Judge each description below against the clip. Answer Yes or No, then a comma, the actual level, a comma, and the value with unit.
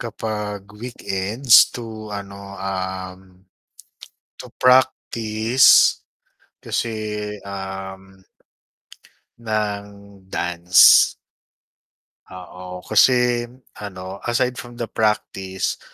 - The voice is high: No, low, 100 Hz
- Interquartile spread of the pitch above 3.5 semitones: No, average, 2.8 semitones